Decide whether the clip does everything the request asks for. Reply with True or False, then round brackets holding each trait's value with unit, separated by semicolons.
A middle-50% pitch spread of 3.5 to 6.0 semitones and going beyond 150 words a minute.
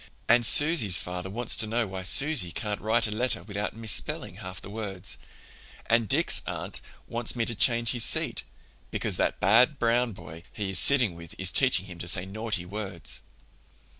True (3.9 semitones; 180 wpm)